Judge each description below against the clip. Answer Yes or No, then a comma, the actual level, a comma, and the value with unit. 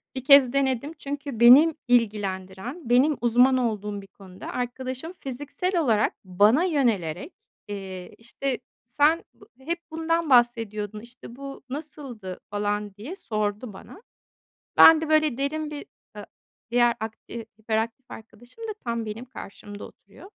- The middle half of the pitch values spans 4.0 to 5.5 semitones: Yes, average, 5.2 semitones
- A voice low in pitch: No, high, 240 Hz